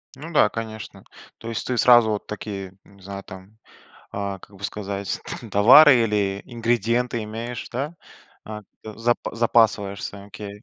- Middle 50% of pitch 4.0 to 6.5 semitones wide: No, average, 2.8 semitones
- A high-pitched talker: No, low, 110 Hz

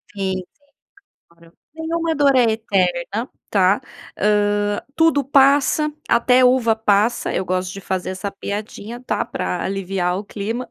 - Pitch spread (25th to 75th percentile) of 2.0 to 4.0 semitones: No, average, 5.0 semitones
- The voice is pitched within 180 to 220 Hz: Yes, high, 210 Hz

